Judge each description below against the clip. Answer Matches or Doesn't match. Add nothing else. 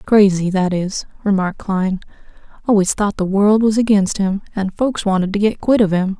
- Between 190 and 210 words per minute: Matches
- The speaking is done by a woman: Matches